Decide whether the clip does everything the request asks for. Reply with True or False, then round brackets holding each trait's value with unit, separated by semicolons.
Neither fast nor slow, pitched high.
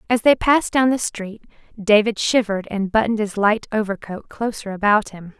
True (180 wpm; 215 Hz)